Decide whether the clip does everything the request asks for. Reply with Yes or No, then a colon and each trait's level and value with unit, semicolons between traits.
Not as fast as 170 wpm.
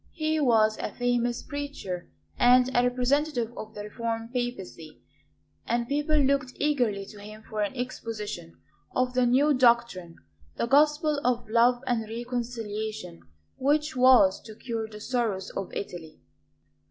Yes: average, 140 wpm